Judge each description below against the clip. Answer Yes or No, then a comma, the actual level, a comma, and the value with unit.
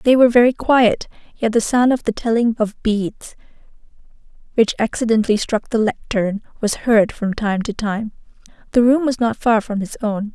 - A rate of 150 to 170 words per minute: No, average, 180 wpm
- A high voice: Yes, high, 225 Hz